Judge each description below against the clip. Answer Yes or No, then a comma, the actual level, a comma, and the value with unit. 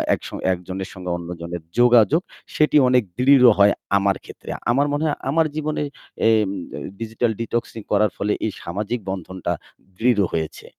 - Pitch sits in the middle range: No, low, 110 Hz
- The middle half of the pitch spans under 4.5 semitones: No, average, 5.2 semitones